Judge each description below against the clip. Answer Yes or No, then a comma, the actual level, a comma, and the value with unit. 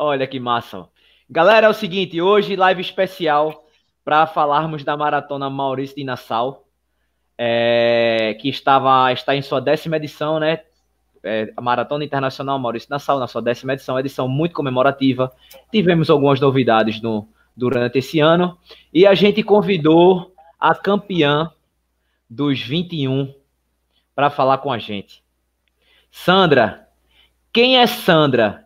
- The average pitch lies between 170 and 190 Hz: No, medium, 140 Hz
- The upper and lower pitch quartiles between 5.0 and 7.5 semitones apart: Yes, wide, 5.4 semitones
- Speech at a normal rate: Yes, average, 135 wpm